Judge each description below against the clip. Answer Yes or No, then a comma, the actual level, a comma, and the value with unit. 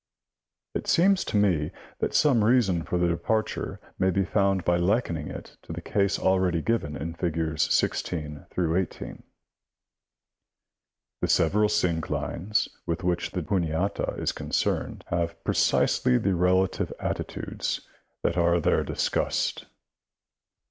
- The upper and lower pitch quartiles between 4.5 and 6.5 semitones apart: No, average, 2.9 semitones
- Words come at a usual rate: No, slow, 125 wpm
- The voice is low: Yes, very low, 90 Hz